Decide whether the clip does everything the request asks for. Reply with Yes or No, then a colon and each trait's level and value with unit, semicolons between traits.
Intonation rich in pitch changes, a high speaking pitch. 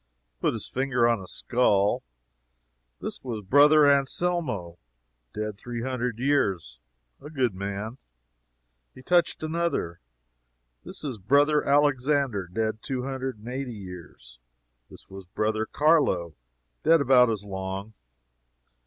No: wide, 6.0 semitones; low, 120 Hz